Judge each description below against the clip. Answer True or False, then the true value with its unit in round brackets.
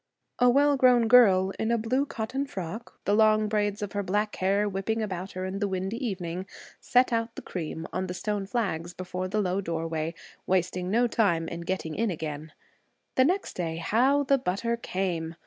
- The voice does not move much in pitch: False (4.1 semitones)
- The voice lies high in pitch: True (200 Hz)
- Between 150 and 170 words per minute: False (190 wpm)